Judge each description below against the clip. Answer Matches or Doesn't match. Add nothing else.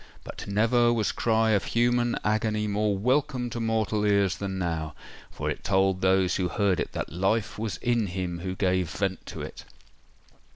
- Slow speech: Doesn't match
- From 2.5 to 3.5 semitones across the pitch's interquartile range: Matches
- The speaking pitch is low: Matches